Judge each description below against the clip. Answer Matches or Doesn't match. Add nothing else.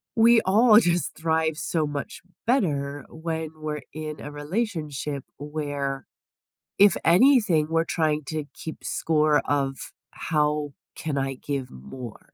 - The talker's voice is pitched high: Doesn't match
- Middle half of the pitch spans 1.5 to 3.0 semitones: Matches